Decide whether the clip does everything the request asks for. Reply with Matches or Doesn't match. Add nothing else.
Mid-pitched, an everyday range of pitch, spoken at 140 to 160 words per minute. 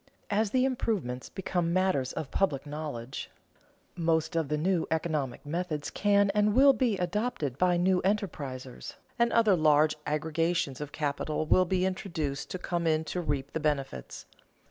Matches